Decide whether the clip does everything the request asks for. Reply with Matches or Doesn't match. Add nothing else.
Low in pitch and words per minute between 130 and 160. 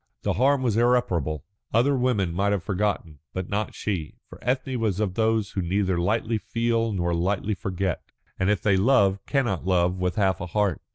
Doesn't match